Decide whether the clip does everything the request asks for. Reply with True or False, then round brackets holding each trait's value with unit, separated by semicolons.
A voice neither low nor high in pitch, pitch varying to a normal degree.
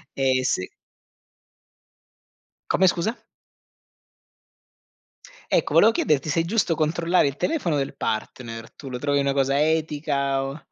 True (145 Hz; 3.5 semitones)